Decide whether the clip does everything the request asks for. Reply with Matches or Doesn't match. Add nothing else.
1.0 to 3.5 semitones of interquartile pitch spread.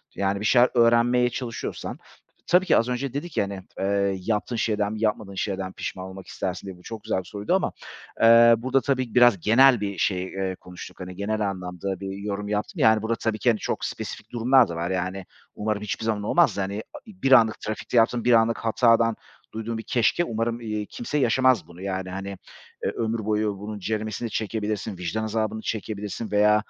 Matches